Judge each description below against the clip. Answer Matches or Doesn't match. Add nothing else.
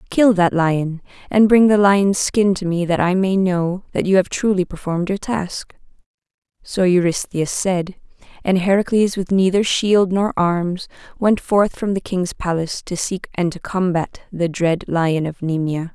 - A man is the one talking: Doesn't match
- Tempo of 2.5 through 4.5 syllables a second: Matches